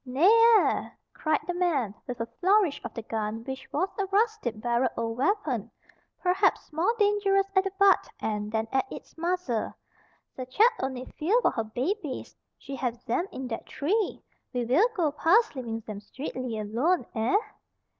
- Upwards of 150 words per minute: Yes, average, 170 wpm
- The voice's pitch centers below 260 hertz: No, very high, 275 Hz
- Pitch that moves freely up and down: Yes, wide, 8.6 semitones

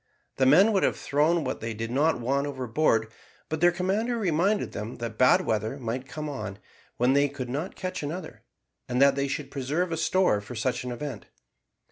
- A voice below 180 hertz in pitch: Yes, medium, 140 Hz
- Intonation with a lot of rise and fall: No, average, 5.0 semitones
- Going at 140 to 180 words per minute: No, average, 195 wpm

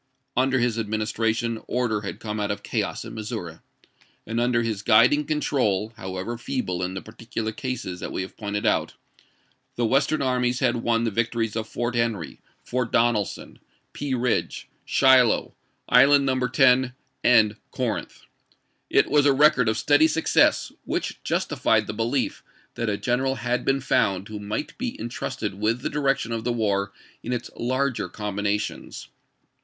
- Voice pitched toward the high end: No, low, 115 Hz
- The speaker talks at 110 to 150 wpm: No, average, 160 wpm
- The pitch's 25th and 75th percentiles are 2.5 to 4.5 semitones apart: Yes, average, 3.1 semitones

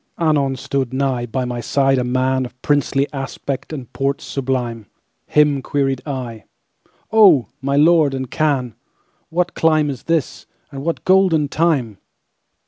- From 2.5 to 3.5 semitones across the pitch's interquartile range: Yes, average, 2.8 semitones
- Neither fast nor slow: No, slow, 120 wpm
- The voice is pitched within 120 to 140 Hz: Yes, low, 135 Hz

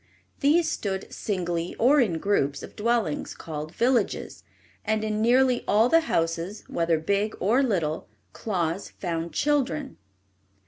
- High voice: Yes, high, 205 Hz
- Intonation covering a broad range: Yes, wide, 6.5 semitones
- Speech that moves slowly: Yes, slow, 130 wpm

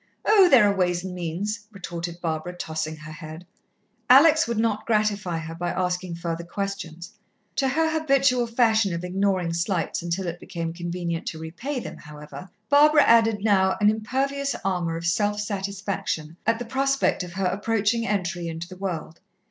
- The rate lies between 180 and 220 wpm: No, average, 165 wpm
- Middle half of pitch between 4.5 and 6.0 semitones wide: Yes, average, 4.9 semitones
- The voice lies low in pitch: No, high, 190 Hz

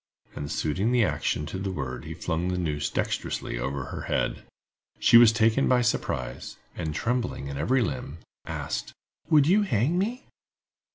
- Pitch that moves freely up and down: Yes, wide, 8.8 semitones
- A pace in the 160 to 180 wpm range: Yes, average, 165 wpm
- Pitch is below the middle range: Yes, low, 100 Hz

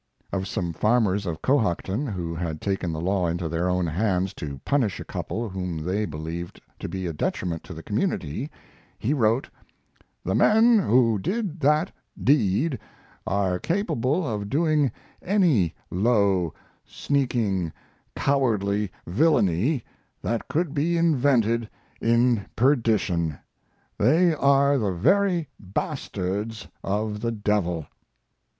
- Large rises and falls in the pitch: Yes, wide, 7.4 semitones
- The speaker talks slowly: Yes, slow, 125 wpm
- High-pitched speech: No, low, 110 Hz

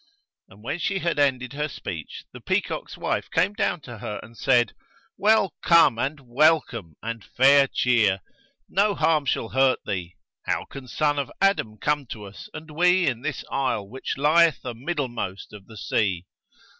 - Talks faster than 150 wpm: Yes, average, 170 wpm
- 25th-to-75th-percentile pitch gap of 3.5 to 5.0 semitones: No, wide, 5.5 semitones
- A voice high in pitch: No, low, 135 Hz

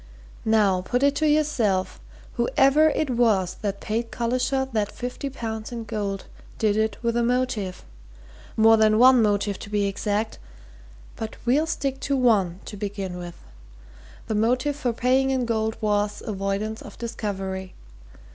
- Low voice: No, high, 220 Hz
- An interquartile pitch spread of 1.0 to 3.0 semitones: No, average, 3.6 semitones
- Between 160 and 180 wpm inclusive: No, average, 150 wpm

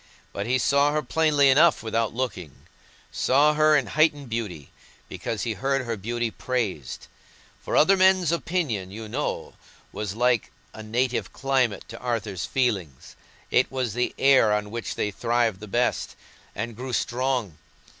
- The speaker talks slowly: No, average, 150 wpm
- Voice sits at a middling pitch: No, low, 120 Hz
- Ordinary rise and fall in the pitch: Yes, average, 4.1 semitones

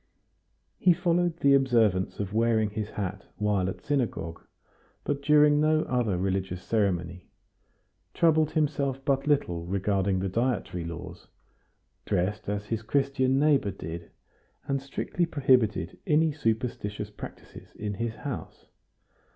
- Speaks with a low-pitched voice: Yes, low, 115 Hz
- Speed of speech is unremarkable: No, slow, 125 wpm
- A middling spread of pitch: No, wide, 6.4 semitones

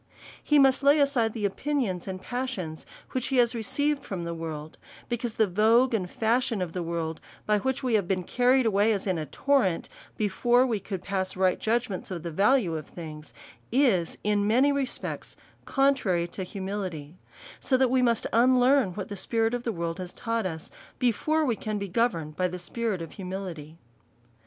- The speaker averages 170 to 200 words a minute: Yes, average, 190 wpm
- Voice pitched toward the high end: Yes, high, 210 Hz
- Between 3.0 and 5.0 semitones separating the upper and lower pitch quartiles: No, wide, 5.5 semitones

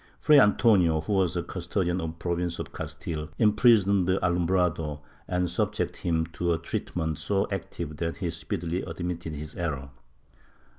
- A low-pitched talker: Yes, very low, 85 Hz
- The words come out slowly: No, average, 150 wpm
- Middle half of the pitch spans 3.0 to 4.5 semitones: No, narrow, 2.4 semitones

